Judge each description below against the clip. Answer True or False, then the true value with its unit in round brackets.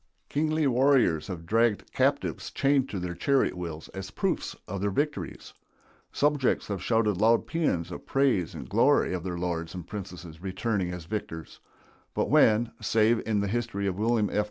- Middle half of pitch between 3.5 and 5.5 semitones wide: True (5.1 semitones)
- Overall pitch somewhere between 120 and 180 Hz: False (105 Hz)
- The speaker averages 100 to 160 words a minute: False (170 wpm)